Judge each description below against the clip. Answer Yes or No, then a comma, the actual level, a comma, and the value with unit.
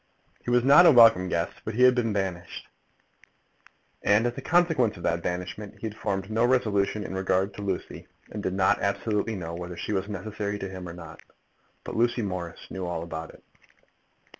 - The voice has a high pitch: No, low, 100 Hz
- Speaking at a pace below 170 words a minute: No, average, 190 wpm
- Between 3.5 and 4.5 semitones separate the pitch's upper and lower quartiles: Yes, average, 3.8 semitones